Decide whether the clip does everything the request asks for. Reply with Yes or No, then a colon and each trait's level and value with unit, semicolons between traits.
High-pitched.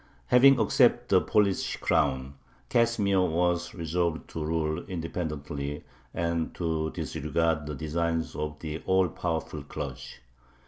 No: very low, 80 Hz